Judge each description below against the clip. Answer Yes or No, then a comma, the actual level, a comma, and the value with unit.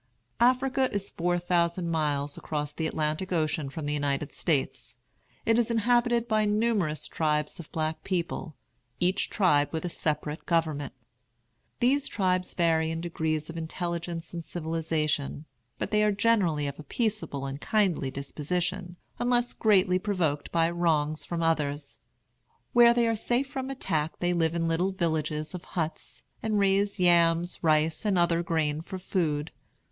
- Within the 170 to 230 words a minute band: No, average, 150 wpm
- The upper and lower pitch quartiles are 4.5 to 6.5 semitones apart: No, average, 4.0 semitones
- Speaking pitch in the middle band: Yes, medium, 170 Hz